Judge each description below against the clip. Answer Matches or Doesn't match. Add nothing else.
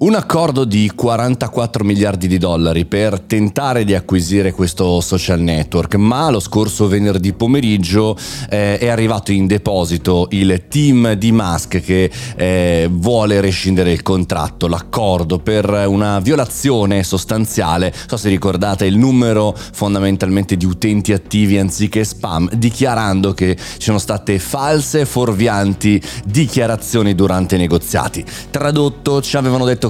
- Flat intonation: Doesn't match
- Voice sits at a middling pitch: Doesn't match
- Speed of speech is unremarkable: Matches